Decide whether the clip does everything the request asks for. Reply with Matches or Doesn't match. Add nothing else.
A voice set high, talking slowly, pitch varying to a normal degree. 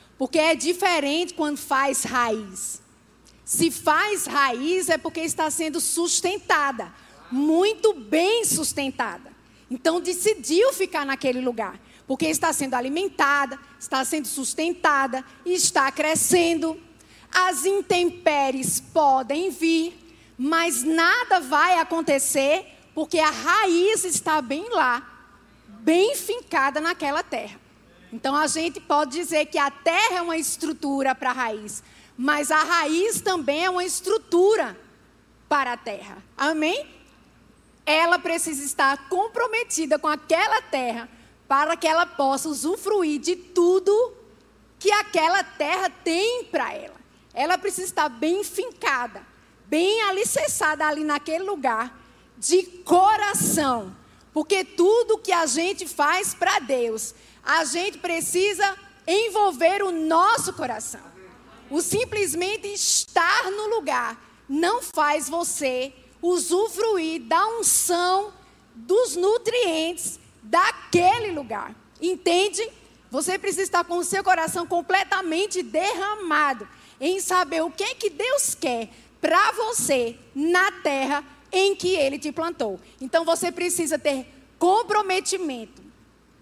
Matches